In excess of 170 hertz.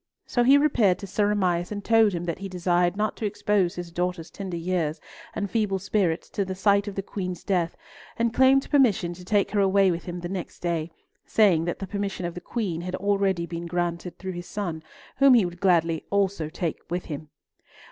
Yes: medium, 185 Hz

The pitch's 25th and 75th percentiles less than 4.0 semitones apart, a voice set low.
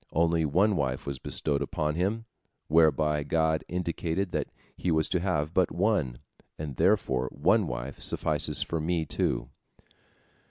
Yes: average, 3.4 semitones; very low, 80 Hz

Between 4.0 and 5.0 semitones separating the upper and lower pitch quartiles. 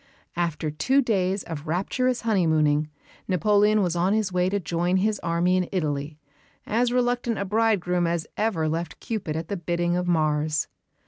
Yes: average, 4.4 semitones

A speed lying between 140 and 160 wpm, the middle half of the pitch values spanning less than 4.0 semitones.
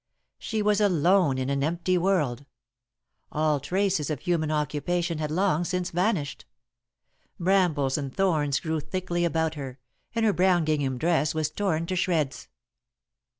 Yes: average, 145 wpm; average, 3.6 semitones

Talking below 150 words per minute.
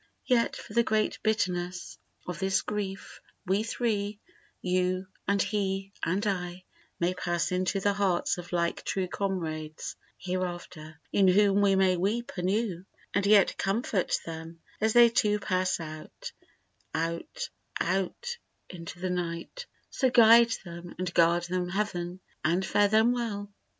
Yes: average, 140 wpm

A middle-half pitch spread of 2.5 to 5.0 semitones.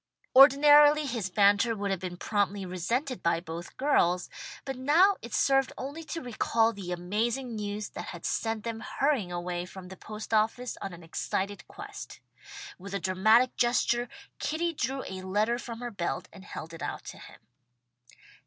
No: wide, 5.5 semitones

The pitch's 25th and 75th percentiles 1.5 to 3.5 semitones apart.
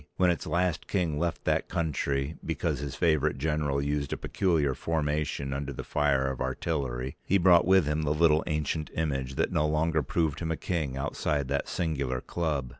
Yes: average, 2.8 semitones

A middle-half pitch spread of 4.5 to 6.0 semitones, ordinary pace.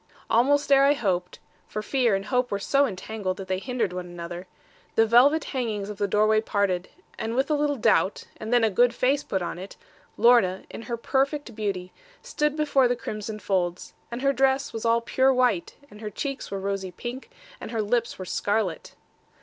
Yes: average, 5.0 semitones; average, 195 wpm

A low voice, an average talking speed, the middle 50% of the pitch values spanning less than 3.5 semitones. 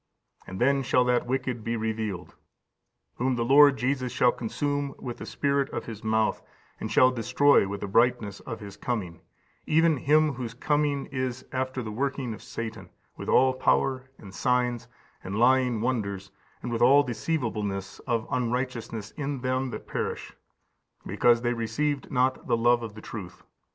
Yes: low, 125 Hz; average, 165 wpm; average, 3.0 semitones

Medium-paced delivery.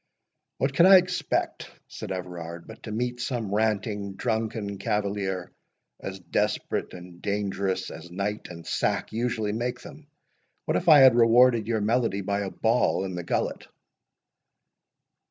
Yes: average, 145 wpm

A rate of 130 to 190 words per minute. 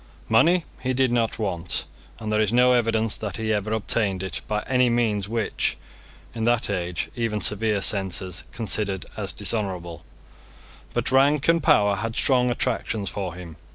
Yes: average, 160 wpm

